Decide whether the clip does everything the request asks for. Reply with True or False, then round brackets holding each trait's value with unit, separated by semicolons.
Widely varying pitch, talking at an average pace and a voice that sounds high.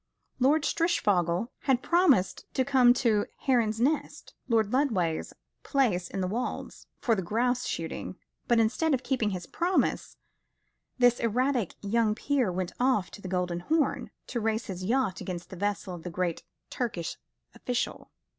True (5.7 semitones; 155 wpm; 225 Hz)